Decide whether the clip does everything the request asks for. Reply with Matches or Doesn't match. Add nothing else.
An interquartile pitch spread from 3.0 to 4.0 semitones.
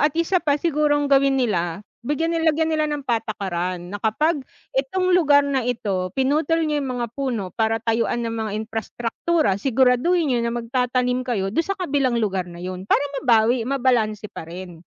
Doesn't match